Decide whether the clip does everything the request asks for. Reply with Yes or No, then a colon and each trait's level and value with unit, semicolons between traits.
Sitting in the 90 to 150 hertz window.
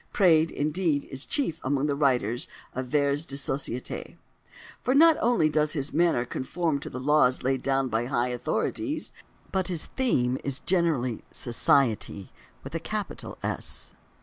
Yes: medium, 140 Hz